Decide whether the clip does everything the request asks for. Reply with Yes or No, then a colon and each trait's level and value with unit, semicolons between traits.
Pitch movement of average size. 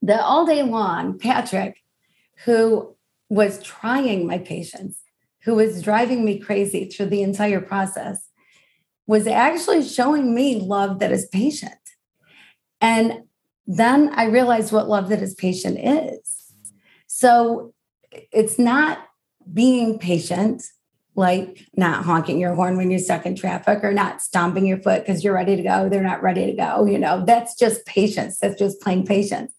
Yes: average, 3.7 semitones